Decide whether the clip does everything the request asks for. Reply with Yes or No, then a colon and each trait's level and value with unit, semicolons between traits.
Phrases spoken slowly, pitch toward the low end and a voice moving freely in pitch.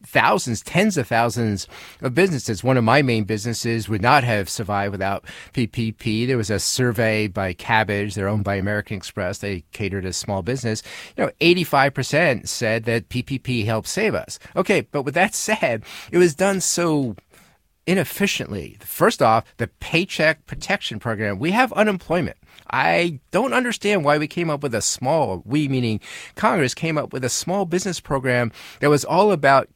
No: average, 170 wpm; low, 125 Hz; wide, 7.3 semitones